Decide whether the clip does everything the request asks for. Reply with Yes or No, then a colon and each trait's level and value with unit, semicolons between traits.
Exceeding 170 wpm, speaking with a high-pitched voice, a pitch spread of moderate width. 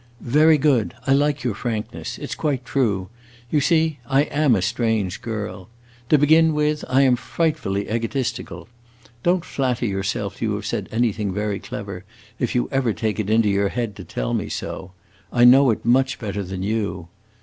No: average, 180 wpm; low, 115 Hz; average, 5.0 semitones